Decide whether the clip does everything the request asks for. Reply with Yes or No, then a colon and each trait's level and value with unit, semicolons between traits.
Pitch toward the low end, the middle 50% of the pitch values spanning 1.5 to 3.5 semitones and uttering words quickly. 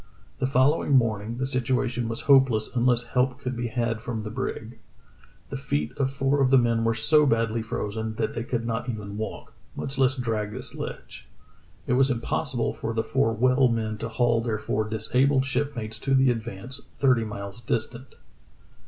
No: low, 120 Hz; average, 2.7 semitones; average, 180 wpm